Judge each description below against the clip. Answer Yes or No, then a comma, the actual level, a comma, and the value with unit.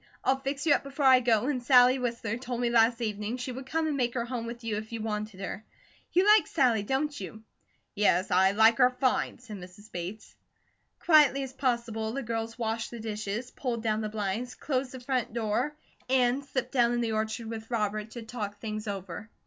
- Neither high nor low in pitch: No, high, 235 Hz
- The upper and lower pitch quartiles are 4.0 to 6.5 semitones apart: No, average, 2.9 semitones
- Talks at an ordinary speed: No, fast, 210 wpm